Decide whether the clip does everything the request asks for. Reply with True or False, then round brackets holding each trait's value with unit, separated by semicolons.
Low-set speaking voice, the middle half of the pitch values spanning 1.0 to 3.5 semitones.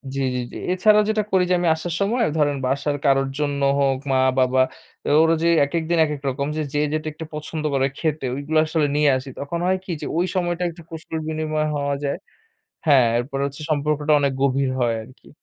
False (150 Hz; 2.8 semitones)